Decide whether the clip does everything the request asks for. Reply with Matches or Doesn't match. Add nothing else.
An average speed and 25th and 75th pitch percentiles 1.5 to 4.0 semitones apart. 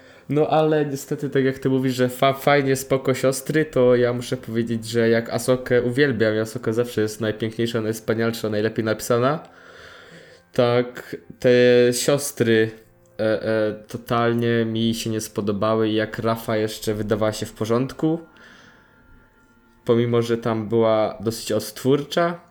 Matches